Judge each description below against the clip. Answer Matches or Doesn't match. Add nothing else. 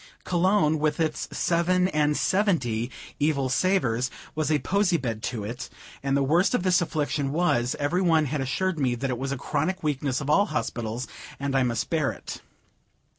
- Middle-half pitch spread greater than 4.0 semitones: Matches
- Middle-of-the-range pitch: Matches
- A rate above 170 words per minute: Matches